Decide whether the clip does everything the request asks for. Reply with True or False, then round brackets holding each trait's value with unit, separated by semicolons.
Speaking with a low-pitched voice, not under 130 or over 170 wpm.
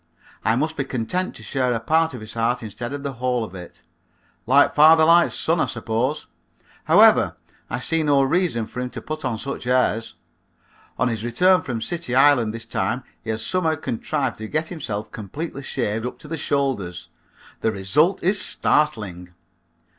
False (130 Hz; 180 wpm)